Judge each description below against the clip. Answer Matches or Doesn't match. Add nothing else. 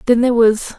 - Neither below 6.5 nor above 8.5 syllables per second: Matches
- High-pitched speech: Matches